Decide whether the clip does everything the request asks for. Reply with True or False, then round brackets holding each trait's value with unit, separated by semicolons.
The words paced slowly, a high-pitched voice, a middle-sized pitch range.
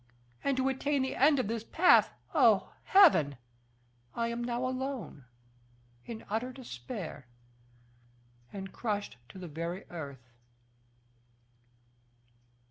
False (110 wpm; 230 Hz; 6.9 semitones)